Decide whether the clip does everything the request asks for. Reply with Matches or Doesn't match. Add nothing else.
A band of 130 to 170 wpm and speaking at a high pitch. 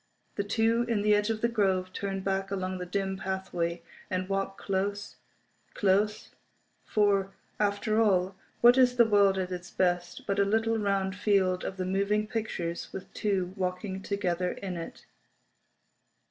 Matches